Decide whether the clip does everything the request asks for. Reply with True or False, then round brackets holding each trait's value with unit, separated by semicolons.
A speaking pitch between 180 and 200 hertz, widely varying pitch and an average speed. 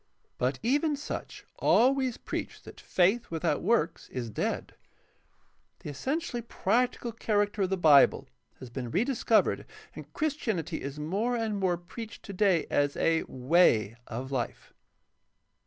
False (190 Hz; 8.2 semitones; 130 wpm)